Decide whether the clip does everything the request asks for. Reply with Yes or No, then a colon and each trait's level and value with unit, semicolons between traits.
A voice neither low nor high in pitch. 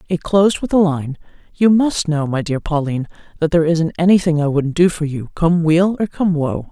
Yes: medium, 165 Hz